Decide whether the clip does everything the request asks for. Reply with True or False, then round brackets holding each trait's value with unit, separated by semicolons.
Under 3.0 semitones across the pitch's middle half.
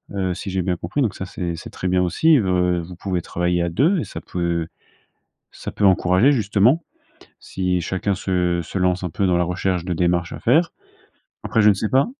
True (2.4 semitones)